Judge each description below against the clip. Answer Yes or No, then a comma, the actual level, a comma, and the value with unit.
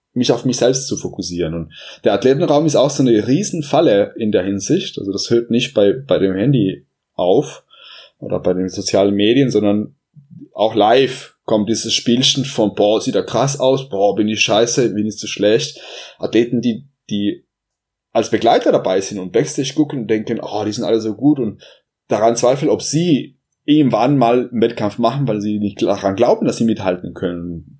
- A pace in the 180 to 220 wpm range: Yes, fast, 190 wpm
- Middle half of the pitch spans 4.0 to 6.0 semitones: Yes, average, 4.8 semitones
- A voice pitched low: Yes, low, 115 Hz